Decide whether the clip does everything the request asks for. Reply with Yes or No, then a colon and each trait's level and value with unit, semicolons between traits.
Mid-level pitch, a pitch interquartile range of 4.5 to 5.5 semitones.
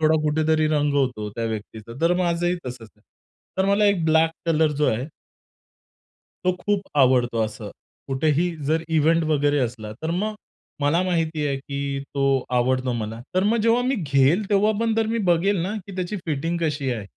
Yes: medium, 155 Hz; average, 5.2 semitones